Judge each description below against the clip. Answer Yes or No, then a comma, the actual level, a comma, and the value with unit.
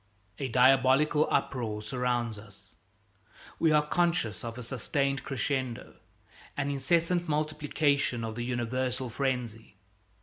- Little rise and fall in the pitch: No, average, 3.5 semitones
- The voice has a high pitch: No, low, 130 Hz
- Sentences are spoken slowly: Yes, slow, 110 wpm